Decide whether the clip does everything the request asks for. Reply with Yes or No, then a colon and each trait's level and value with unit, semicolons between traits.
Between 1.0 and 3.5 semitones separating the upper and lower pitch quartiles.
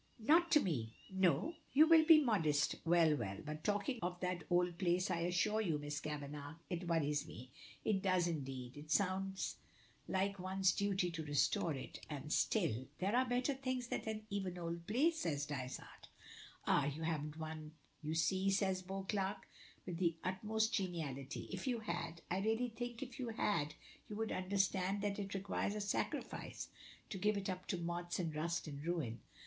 No: average, 4.8 semitones